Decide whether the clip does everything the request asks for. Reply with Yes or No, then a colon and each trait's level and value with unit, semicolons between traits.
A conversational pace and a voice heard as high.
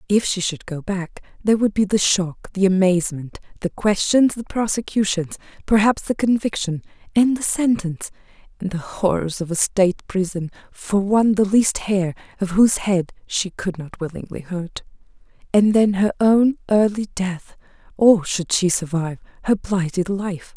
Yes: average, 160 wpm; high, 195 Hz